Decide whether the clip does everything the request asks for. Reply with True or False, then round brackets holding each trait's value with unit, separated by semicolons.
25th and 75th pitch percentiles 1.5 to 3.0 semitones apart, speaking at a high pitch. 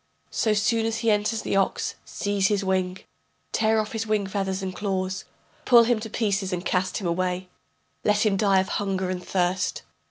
True (2.4 semitones; 195 Hz)